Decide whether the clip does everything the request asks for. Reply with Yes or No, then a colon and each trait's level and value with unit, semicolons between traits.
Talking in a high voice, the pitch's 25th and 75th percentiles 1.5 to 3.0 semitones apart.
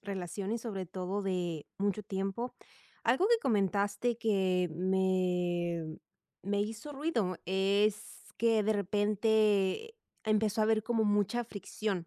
Yes: high, 205 Hz; average, 2.7 semitones